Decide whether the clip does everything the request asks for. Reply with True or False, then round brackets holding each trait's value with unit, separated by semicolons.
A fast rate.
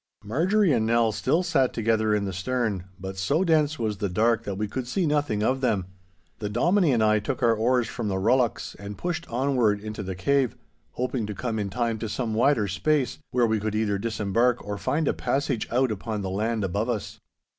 True (210 wpm)